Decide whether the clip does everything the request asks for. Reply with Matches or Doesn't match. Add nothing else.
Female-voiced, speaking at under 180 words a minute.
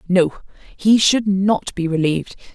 Matches